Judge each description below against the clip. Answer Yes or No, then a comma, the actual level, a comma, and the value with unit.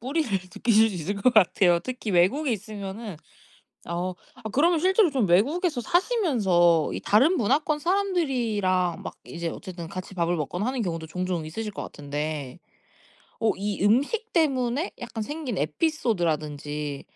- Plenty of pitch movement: Yes, wide, 8.1 semitones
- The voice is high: Yes, high, 210 Hz